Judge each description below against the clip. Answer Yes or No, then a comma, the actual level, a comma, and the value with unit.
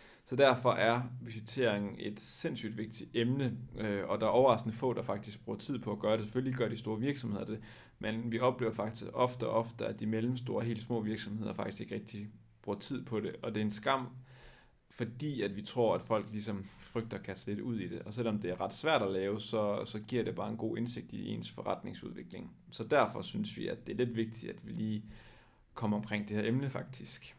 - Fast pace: Yes, fast, 230 wpm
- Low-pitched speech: Yes, low, 110 Hz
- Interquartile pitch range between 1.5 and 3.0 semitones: Yes, narrow, 2.4 semitones